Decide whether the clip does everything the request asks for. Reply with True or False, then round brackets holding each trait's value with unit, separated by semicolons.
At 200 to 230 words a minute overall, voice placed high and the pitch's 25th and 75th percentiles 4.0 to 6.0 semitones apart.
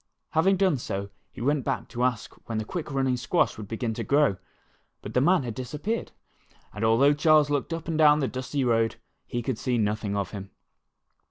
False (205 wpm; 130 Hz; 4.8 semitones)